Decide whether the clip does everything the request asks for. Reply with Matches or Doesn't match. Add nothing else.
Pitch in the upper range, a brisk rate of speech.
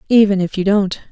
Matches